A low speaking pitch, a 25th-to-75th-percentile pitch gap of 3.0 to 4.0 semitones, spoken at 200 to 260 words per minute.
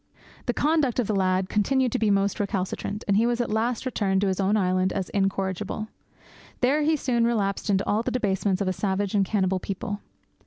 No: high, 205 Hz; average, 3.5 semitones; fast, 205 wpm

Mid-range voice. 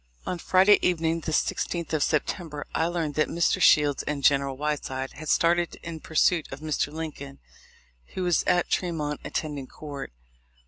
Yes: medium, 155 Hz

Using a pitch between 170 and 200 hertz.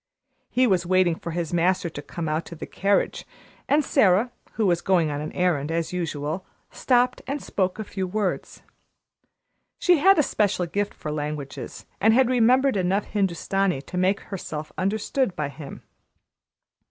Yes: medium, 185 Hz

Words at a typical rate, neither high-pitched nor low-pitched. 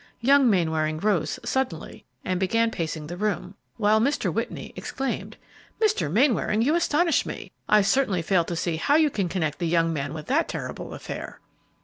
No: average, 170 wpm; high, 195 Hz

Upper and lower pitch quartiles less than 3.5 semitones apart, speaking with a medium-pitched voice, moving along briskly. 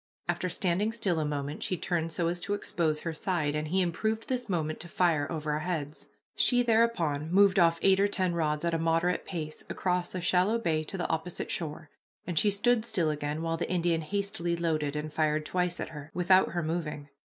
Yes: average, 3.1 semitones; medium, 170 Hz; fast, 210 wpm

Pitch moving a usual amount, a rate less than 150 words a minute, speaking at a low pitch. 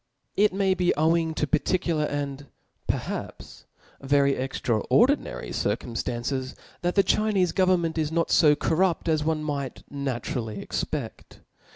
No: average, 4.2 semitones; average, 140 wpm; medium, 155 Hz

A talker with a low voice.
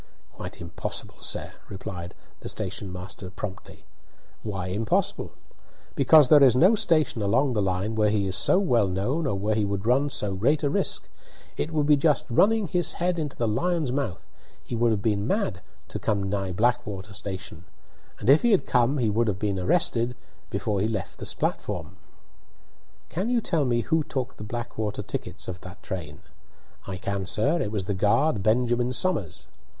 Yes: low, 110 Hz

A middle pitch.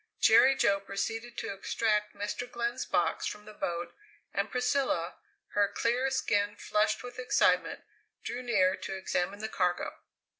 No: high, 210 Hz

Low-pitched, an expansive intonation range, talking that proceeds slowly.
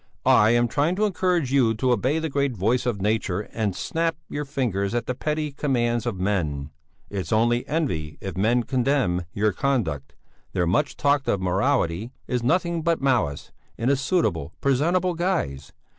No: low, 120 Hz; wide, 6.6 semitones; average, 170 wpm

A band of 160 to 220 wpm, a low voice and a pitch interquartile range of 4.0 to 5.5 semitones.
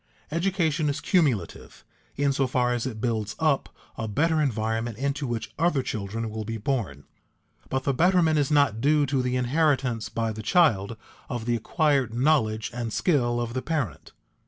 Yes: average, 170 wpm; low, 125 Hz; average, 4.7 semitones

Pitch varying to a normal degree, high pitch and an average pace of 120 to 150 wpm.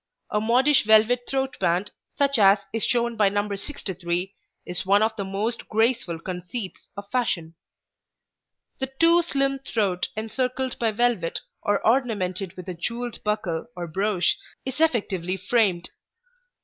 Yes: average, 4.7 semitones; high, 210 Hz; average, 140 wpm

